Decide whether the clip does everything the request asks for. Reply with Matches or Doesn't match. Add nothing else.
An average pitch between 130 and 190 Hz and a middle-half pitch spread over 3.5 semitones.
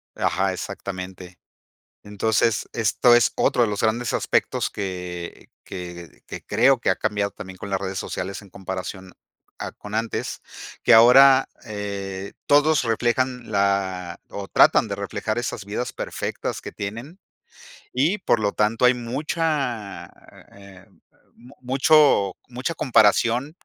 Doesn't match